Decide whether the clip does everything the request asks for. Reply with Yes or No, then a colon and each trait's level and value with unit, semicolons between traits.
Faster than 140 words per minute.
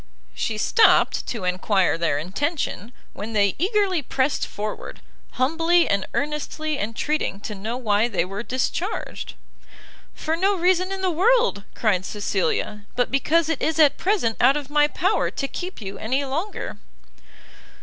Yes: average, 150 wpm